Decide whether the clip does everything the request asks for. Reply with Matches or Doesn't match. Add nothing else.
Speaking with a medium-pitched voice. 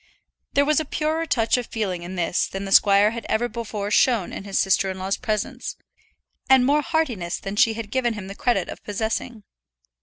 Doesn't match